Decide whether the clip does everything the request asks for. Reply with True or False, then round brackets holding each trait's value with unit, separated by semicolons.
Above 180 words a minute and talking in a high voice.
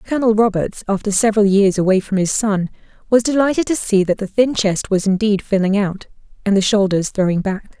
True (200 wpm; 205 Hz)